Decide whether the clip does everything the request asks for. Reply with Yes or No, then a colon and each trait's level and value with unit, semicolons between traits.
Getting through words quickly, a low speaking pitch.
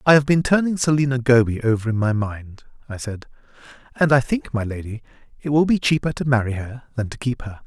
Yes: fast, 220 wpm; low, 125 Hz